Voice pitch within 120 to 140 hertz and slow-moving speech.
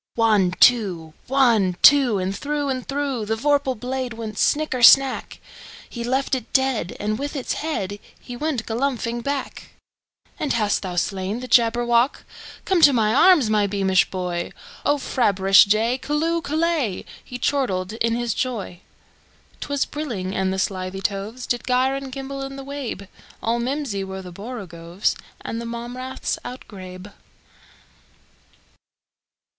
No: high, 235 Hz; slow, 125 wpm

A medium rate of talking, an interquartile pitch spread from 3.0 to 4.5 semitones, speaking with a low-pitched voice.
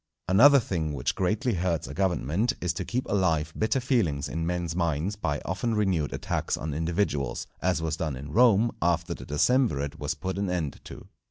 No: average, 185 wpm; average, 4.9 semitones; very low, 85 Hz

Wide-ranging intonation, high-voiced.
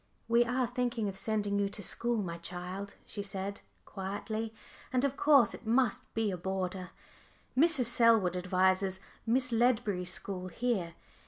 No: average, 4.1 semitones; high, 205 Hz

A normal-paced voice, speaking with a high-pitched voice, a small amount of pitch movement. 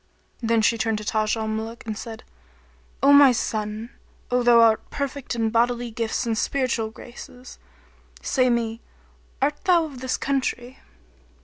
Yes: average, 155 wpm; high, 235 Hz; narrow, 2.3 semitones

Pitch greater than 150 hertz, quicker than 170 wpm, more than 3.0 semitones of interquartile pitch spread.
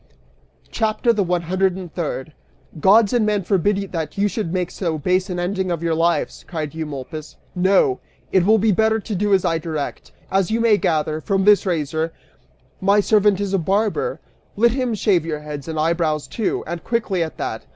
Yes: medium, 185 Hz; average, 195 wpm; average, 4.2 semitones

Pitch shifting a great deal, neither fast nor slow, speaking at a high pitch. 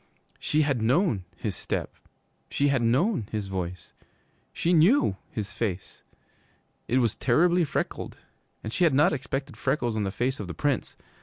No: wide, 6.2 semitones; average, 160 wpm; low, 130 Hz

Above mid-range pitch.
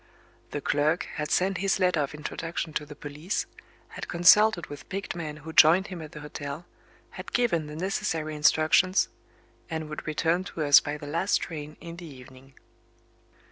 No: medium, 155 Hz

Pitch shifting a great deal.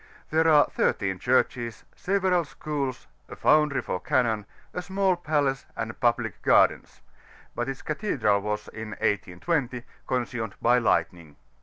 Yes: wide, 5.9 semitones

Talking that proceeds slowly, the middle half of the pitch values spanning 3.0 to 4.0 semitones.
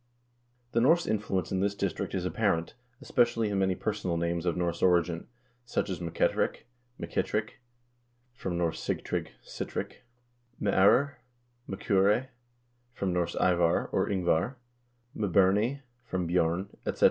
Yes: slow, 125 wpm; average, 3.4 semitones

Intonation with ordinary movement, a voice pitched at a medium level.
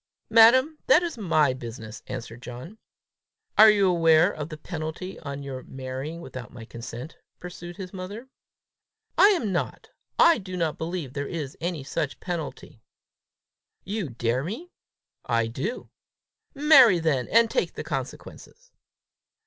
No: wide, 8.0 semitones; medium, 165 Hz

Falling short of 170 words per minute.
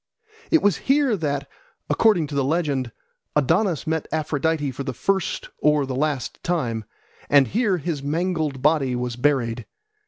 Yes: average, 150 wpm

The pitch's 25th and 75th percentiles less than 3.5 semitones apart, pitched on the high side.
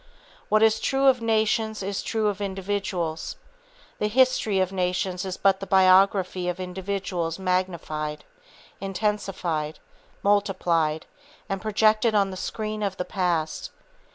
Yes: average, 2.7 semitones; high, 195 Hz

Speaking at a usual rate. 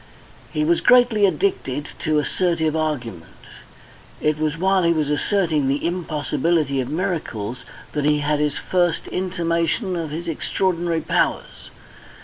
No: slow, 130 wpm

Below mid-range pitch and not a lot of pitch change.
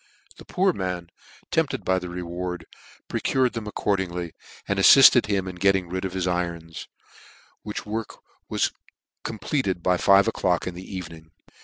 Yes: very low, 95 Hz; narrow, 2.3 semitones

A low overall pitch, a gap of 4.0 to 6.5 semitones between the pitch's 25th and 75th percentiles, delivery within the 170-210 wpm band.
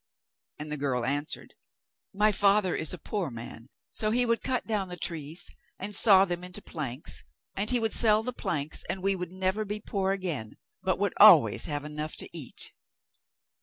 No: medium, 185 Hz; wide, 5.6 semitones; average, 185 wpm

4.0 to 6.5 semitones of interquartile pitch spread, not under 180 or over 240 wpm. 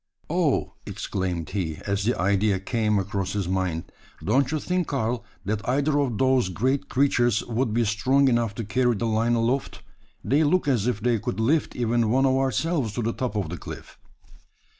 Yes: average, 4.5 semitones; average, 185 wpm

